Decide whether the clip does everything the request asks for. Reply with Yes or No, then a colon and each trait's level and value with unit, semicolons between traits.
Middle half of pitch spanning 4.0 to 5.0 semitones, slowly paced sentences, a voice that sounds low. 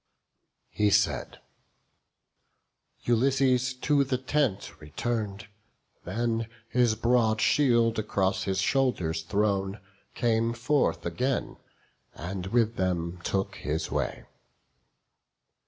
Yes: average, 4.4 semitones; slow, 90 wpm; low, 115 Hz